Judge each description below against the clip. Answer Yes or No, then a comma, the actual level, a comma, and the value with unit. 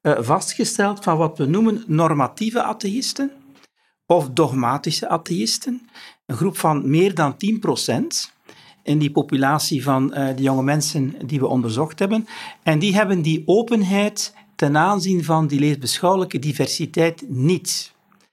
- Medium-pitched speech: Yes, medium, 165 Hz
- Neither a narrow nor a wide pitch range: No, wide, 5.8 semitones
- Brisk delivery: No, slow, 130 wpm